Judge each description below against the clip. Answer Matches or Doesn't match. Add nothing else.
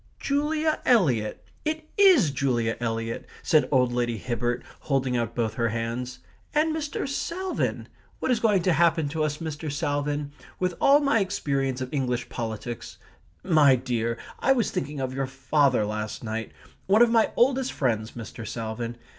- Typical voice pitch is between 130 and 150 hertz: Matches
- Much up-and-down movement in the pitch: Matches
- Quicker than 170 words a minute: Doesn't match